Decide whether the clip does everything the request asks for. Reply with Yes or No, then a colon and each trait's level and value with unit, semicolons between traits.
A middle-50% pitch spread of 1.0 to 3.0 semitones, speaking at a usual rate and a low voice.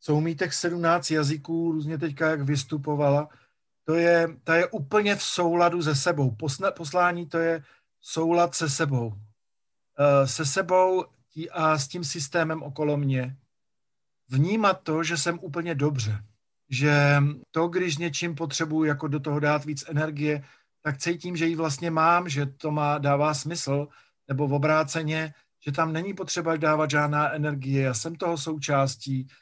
No: narrow, 2.6 semitones; average, 150 wpm; medium, 155 Hz